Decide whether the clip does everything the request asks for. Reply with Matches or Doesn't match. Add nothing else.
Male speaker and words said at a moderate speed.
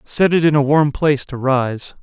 Doesn't match